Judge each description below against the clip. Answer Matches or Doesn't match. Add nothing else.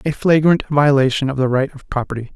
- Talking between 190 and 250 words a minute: Matches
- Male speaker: Matches